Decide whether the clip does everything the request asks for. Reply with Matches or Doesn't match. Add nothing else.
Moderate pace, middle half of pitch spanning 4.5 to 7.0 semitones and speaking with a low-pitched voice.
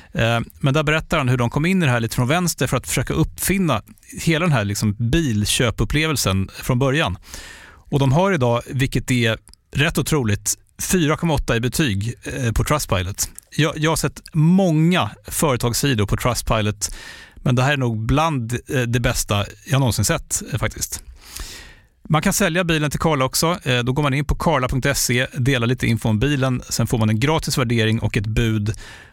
Matches